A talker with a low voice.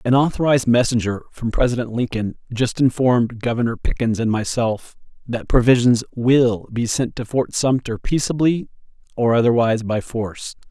Yes: low, 120 Hz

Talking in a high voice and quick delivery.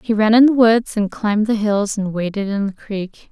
Yes: high, 210 Hz; fast, 255 wpm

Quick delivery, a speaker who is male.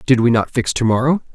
Yes: fast, 265 wpm; male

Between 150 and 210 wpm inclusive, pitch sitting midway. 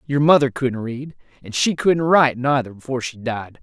No: average, 200 wpm; low, 130 Hz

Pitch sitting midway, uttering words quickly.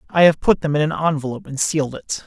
Yes: medium, 150 Hz; fast, 265 wpm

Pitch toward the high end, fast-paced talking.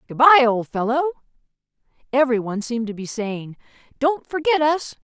No: very high, 260 Hz; average, 155 wpm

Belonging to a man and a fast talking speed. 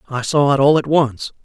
Yes: male; fast, 250 wpm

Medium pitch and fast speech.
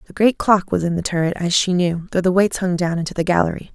Yes: medium, 180 Hz; fast, 290 wpm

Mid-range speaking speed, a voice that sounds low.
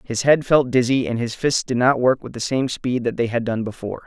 No: fast, 280 wpm; low, 120 Hz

